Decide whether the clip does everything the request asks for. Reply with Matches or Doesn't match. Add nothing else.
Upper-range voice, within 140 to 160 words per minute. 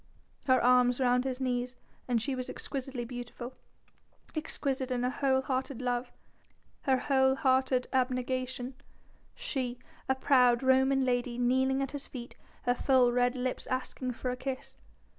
Matches